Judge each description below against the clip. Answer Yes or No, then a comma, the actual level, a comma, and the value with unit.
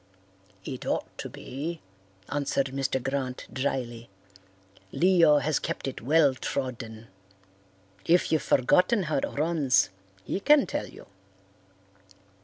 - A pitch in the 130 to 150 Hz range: Yes, medium, 140 Hz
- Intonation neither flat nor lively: Yes, average, 4.0 semitones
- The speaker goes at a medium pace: No, slow, 115 wpm